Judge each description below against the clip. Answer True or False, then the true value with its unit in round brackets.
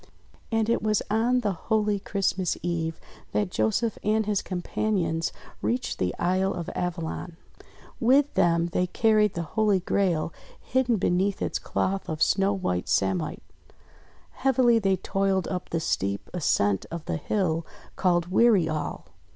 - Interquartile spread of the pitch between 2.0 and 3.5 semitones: False (4.1 semitones)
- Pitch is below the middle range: False (190 Hz)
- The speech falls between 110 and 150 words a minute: True (145 wpm)